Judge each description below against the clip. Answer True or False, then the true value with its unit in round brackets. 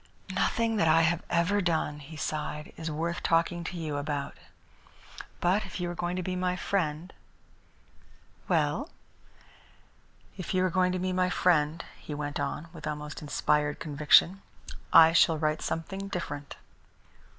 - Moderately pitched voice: True (165 Hz)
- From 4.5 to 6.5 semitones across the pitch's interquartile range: False (3.2 semitones)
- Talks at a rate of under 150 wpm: False (155 wpm)